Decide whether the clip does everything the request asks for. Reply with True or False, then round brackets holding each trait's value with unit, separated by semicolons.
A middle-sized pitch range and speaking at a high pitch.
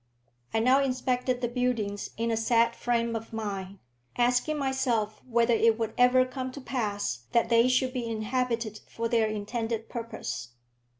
False (2.2 semitones; 230 Hz)